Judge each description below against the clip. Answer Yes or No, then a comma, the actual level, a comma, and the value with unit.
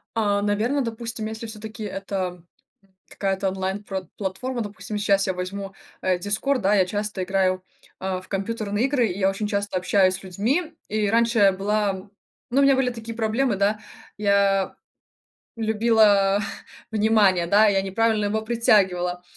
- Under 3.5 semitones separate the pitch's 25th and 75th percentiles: Yes, narrow, 2.4 semitones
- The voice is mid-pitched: No, high, 205 Hz